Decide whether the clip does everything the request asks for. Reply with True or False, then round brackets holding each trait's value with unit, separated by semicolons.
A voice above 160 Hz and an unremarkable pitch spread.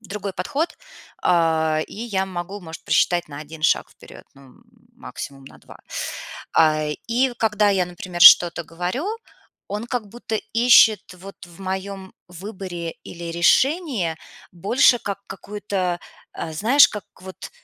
True (190 Hz; 3.8 semitones)